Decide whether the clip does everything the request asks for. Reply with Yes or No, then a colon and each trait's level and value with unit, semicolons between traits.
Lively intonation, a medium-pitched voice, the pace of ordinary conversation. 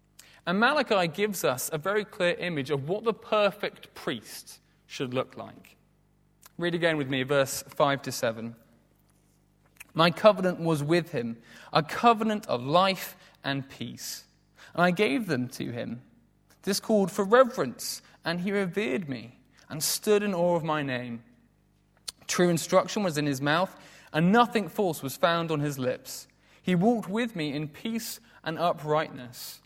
Yes: wide, 6.0 semitones; medium, 170 Hz; average, 160 wpm